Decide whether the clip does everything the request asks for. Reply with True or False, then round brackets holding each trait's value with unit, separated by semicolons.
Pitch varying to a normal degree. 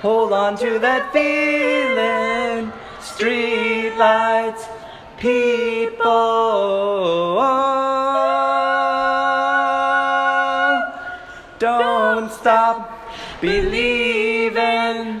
True (3.1 semitones)